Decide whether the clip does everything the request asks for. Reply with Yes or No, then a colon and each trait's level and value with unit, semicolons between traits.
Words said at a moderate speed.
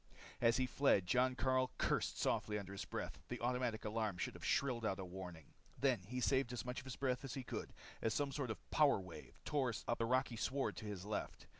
No: fast, 230 wpm